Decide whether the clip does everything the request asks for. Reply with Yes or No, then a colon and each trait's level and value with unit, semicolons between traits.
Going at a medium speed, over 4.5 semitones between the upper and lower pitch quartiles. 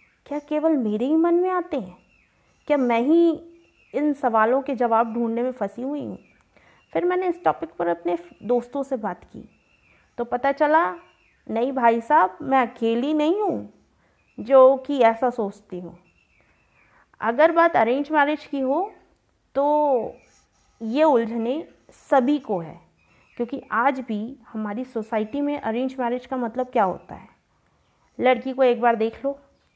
No: average, 155 wpm; average, 4.2 semitones